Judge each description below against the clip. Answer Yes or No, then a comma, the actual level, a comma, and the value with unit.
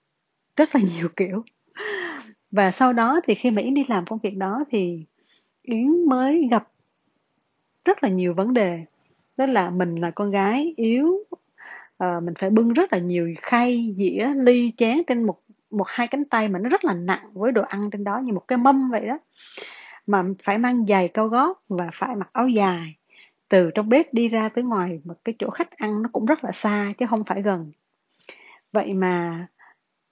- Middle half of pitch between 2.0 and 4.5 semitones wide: No, average, 4.9 semitones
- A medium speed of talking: Yes, average, 195 wpm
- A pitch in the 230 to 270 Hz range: No, high, 220 Hz